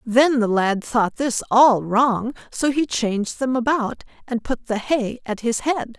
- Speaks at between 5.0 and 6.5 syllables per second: No, 3.9 syllables/s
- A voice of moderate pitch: No, high, 240 Hz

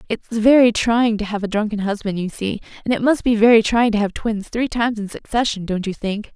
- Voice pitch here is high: Yes, high, 220 Hz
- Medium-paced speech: No, fast, 245 wpm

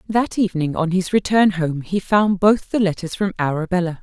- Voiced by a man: No, female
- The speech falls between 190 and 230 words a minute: Yes, average, 195 wpm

